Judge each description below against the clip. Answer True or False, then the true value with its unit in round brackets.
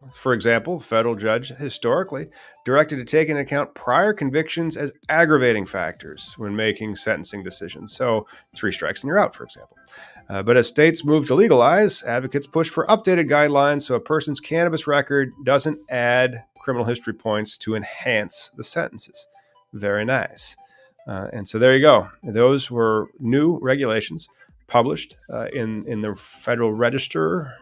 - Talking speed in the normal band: True (160 wpm)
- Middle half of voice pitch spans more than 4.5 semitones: True (5.3 semitones)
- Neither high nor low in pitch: False (130 Hz)